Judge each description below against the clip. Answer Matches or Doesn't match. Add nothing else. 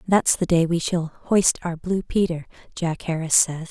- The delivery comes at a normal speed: Matches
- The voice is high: Doesn't match